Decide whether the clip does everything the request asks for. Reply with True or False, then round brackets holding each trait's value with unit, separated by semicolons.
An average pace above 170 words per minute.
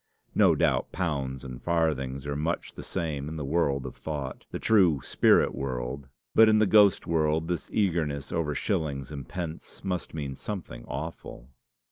False (165 wpm)